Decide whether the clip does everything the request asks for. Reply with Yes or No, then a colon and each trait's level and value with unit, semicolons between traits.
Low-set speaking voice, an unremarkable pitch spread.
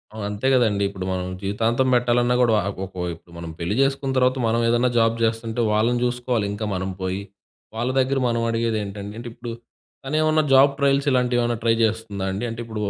Yes: low, 115 Hz; average, 3.1 semitones